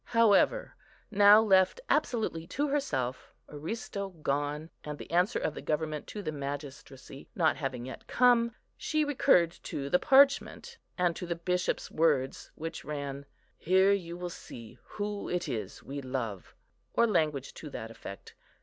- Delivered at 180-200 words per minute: No, average, 150 wpm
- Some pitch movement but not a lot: No, wide, 6.5 semitones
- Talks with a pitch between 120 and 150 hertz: No, medium, 165 Hz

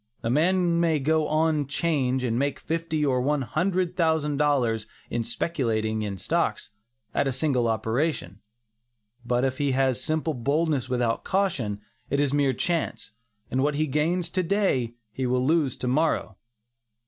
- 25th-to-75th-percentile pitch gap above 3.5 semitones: Yes, average, 4.4 semitones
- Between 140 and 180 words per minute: Yes, average, 160 wpm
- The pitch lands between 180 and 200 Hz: No, medium, 140 Hz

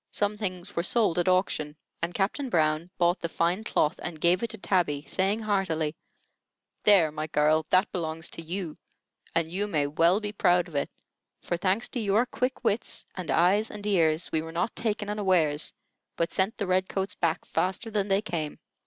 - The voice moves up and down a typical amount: Yes, average, 4.0 semitones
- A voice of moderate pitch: Yes, medium, 180 Hz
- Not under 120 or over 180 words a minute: No, average, 190 wpm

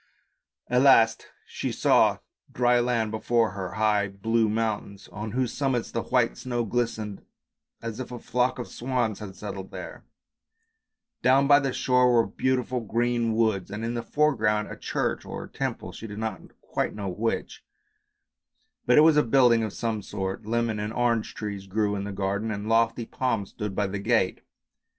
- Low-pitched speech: Yes, low, 115 Hz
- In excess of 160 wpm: Yes, average, 175 wpm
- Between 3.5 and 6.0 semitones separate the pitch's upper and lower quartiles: No, average, 2.7 semitones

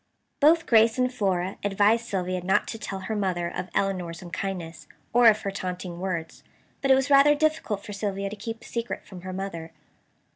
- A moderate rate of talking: Yes, average, 190 wpm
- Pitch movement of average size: Yes, average, 3.8 semitones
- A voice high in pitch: Yes, high, 195 Hz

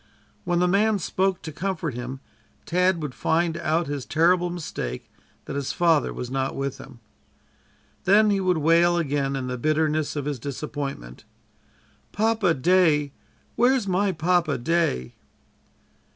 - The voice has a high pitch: No, medium, 160 Hz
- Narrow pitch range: No, average, 4.5 semitones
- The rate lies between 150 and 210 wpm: No, average, 140 wpm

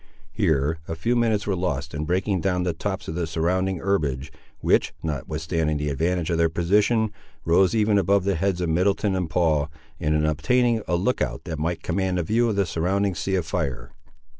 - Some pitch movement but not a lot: Yes, average, 3.7 semitones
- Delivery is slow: No, average, 200 wpm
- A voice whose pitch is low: Yes, very low, 90 Hz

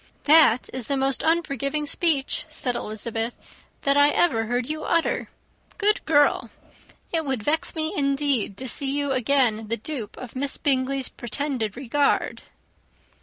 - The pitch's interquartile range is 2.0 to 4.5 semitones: Yes, average, 3.3 semitones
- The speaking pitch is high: Yes, very high, 275 Hz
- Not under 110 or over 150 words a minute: Yes, average, 145 wpm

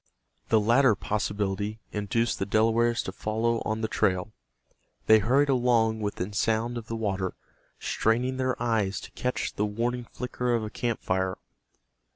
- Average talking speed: Yes, average, 155 wpm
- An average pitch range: No, narrow, 2.3 semitones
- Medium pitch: No, low, 110 Hz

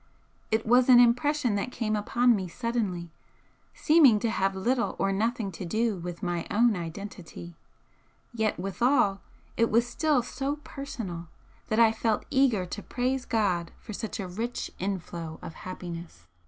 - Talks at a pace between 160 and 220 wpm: No, average, 150 wpm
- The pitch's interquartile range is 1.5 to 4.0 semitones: No, average, 4.7 semitones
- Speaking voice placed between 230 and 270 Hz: No, high, 215 Hz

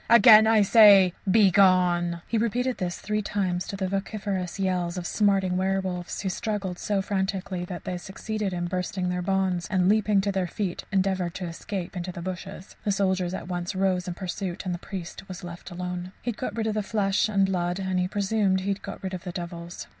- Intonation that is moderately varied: No, narrow, 2.0 semitones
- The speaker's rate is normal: No, fast, 215 wpm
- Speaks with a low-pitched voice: No, high, 190 Hz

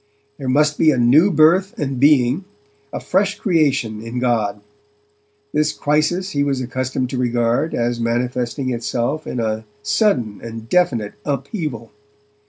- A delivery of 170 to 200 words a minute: No, average, 140 wpm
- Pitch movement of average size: Yes, average, 4.4 semitones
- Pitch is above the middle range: No, low, 130 Hz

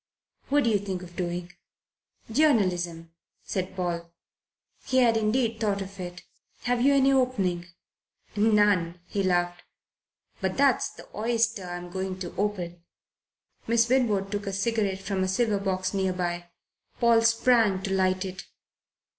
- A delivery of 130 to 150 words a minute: Yes, average, 145 wpm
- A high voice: Yes, high, 195 Hz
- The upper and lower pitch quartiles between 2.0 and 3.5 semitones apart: No, average, 3.9 semitones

